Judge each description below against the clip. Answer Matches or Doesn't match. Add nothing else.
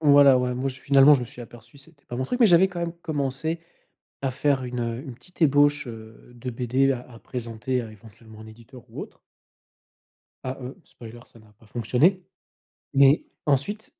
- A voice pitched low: Matches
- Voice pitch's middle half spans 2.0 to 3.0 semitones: Doesn't match